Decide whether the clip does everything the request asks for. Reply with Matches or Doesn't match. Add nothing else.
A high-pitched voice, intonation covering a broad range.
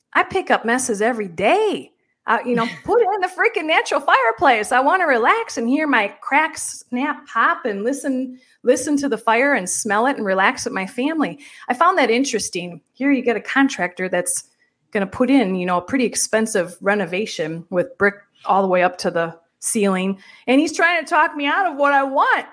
Matches